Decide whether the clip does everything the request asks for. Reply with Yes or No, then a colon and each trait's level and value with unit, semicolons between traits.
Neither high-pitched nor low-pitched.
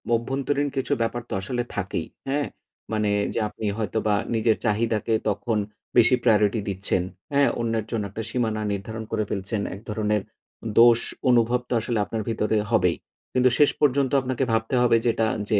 No: low, 115 Hz